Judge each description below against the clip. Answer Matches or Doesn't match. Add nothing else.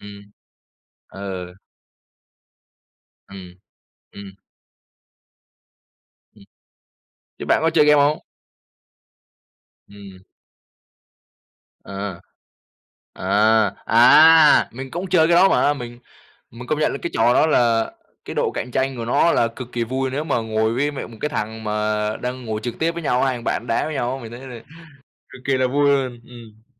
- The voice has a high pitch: Doesn't match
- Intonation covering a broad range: Doesn't match